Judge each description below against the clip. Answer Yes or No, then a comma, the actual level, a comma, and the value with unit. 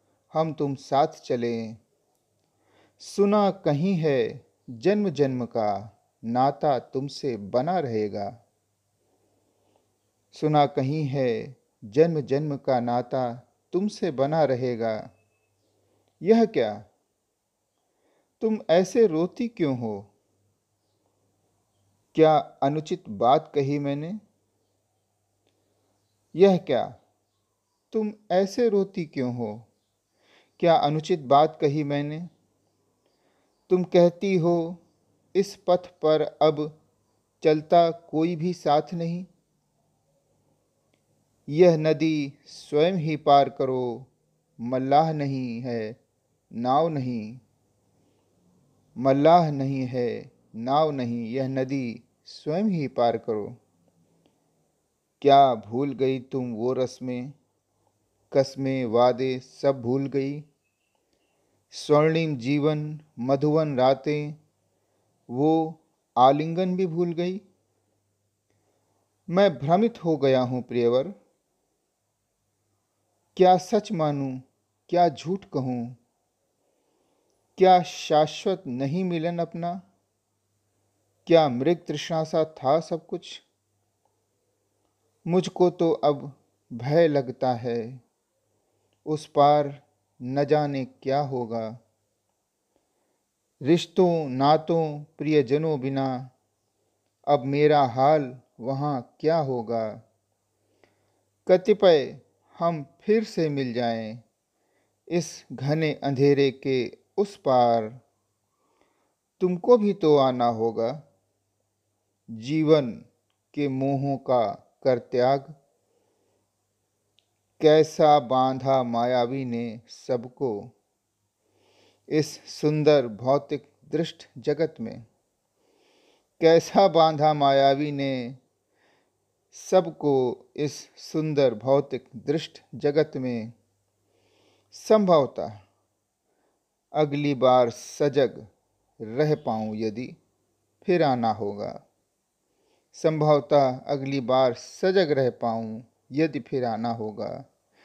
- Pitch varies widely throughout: Yes, wide, 5.8 semitones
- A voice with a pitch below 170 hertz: Yes, low, 135 Hz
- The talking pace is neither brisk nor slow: No, slow, 85 wpm